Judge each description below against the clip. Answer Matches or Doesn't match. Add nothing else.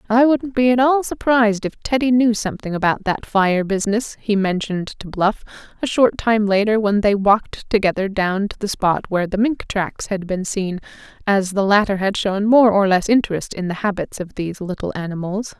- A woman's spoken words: Matches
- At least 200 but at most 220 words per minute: Matches